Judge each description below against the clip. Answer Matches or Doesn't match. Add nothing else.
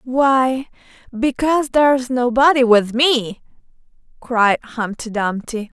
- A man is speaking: Doesn't match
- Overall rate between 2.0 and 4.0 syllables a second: Matches